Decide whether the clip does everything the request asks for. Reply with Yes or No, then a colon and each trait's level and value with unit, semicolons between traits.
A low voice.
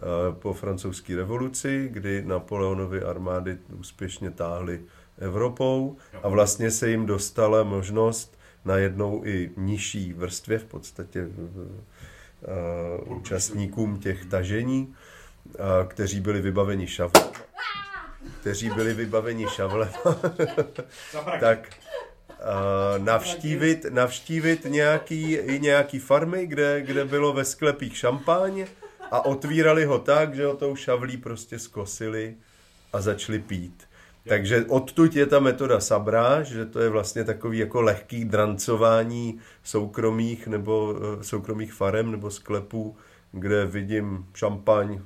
Yes: low, 110 Hz